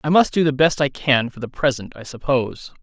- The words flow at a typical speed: No, fast, 255 wpm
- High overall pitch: No, low, 135 Hz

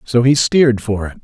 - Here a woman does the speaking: No, male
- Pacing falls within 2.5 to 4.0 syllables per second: No, 5.5 syllables/s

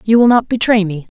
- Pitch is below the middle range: No, high, 215 Hz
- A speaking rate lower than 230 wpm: No, fast, 250 wpm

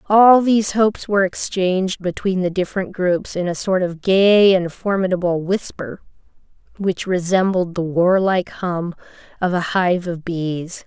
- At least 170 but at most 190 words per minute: No, average, 150 wpm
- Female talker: Yes, female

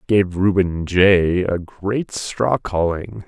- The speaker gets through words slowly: Yes, slow, 110 wpm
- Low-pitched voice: Yes, very low, 95 Hz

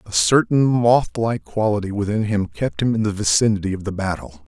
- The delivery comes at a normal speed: Yes, average, 185 wpm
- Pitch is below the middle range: Yes, low, 105 Hz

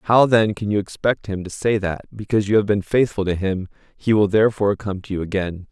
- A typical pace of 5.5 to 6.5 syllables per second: Yes, 5.8 syllables/s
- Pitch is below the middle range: Yes, low, 100 Hz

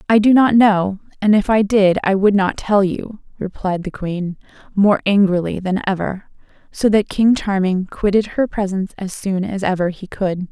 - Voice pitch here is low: No, high, 195 Hz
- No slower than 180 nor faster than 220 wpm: Yes, average, 190 wpm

